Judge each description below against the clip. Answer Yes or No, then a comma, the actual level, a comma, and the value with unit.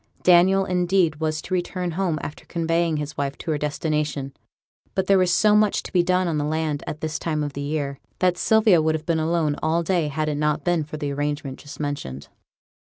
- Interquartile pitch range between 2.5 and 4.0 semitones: Yes, average, 3.1 semitones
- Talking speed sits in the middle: No, fast, 220 wpm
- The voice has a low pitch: No, medium, 155 Hz